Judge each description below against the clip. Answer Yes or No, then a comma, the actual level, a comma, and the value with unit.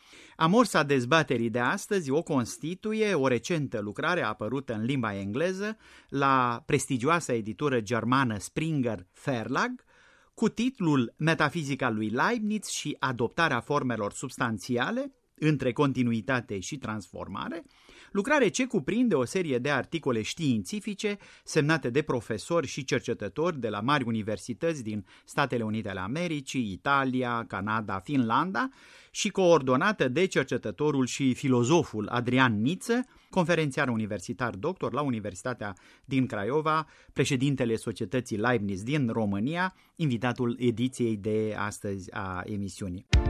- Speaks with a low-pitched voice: Yes, low, 130 Hz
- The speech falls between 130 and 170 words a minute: No, slow, 115 wpm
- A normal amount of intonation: No, wide, 6.1 semitones